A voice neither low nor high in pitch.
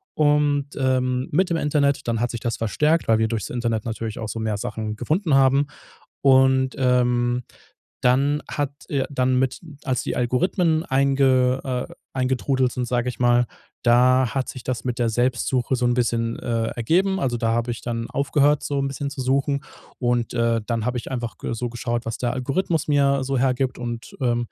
No: low, 125 Hz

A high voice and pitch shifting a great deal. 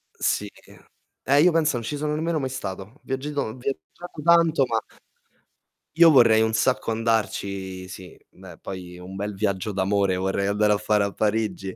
No: low, 110 Hz; wide, 6.0 semitones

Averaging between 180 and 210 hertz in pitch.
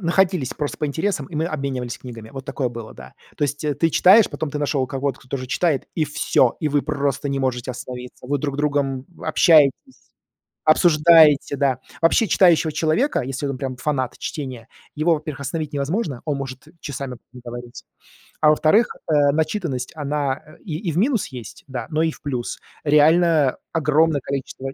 No: medium, 145 Hz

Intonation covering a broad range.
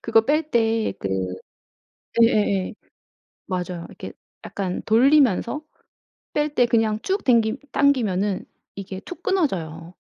Yes: wide, 6.6 semitones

